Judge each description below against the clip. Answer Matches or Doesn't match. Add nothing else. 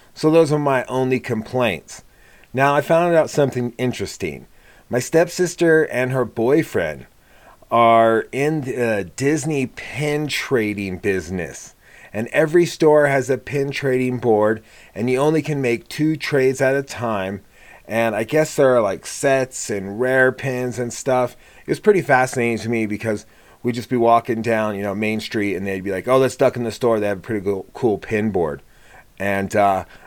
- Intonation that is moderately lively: Matches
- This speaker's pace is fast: Doesn't match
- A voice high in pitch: Doesn't match